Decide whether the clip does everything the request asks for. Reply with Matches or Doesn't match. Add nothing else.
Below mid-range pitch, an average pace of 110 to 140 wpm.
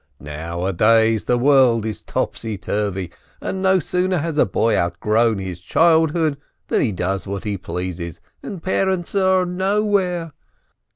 Matches